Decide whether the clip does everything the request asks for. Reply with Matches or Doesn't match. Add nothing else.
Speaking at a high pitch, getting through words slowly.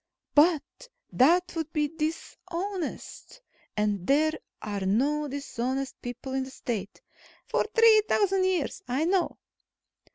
Matches